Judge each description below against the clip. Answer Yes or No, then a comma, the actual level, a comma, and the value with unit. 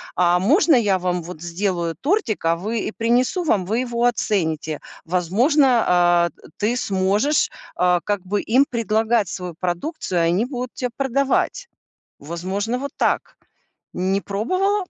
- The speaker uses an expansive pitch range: Yes, wide, 5.8 semitones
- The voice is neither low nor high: No, high, 205 Hz